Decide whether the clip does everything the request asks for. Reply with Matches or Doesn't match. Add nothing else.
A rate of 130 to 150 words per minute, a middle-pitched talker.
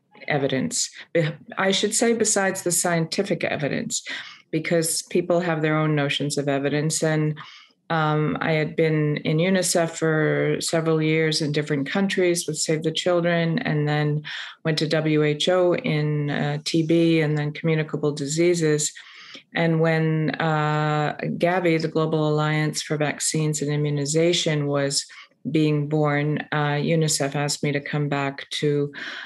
Matches